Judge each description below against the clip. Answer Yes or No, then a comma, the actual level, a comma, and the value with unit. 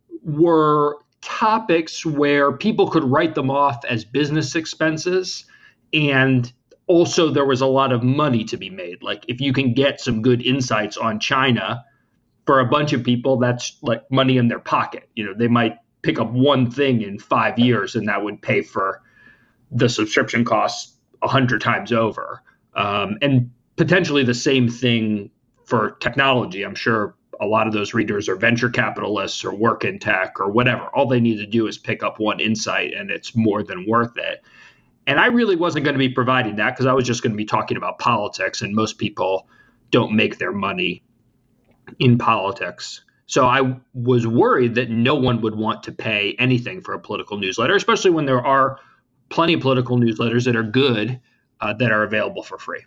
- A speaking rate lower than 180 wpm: No, average, 190 wpm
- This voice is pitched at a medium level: No, low, 125 Hz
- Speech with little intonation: No, average, 3.3 semitones